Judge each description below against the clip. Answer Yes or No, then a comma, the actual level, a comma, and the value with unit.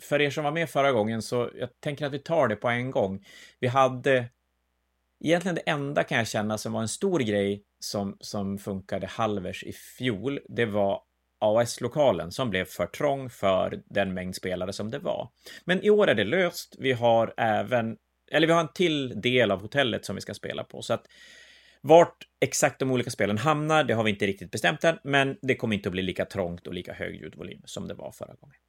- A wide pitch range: Yes, wide, 6.3 semitones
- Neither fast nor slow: No, fast, 220 wpm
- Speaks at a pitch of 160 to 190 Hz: No, low, 120 Hz